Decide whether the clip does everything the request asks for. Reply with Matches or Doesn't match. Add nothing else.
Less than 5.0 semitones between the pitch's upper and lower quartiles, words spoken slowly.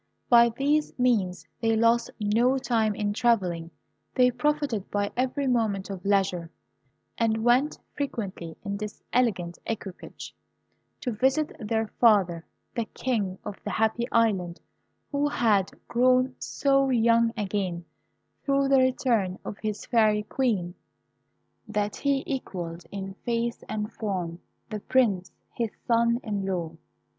Matches